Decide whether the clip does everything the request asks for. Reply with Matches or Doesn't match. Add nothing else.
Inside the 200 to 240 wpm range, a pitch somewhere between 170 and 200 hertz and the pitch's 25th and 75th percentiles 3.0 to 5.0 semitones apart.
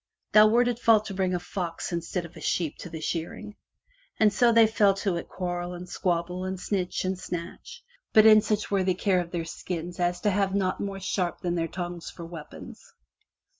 Doesn't match